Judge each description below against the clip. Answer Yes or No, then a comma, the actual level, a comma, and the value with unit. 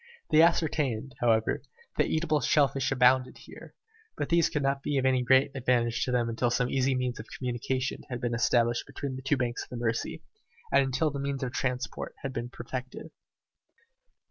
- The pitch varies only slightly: Yes, narrow, 2.2 semitones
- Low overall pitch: Yes, low, 130 Hz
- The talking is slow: No, average, 190 wpm